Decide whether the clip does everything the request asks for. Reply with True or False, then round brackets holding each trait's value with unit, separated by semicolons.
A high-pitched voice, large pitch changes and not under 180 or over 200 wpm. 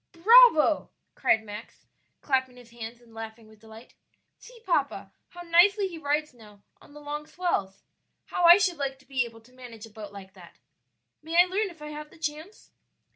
True (285 Hz; 7.1 semitones; 190 wpm)